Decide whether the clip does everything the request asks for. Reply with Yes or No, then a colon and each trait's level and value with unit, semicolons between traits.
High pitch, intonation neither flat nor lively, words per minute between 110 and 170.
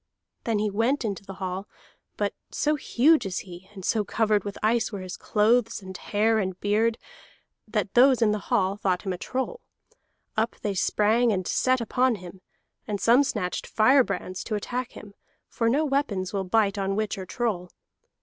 No: high, 210 Hz; average, 3.5 semitones; average, 180 wpm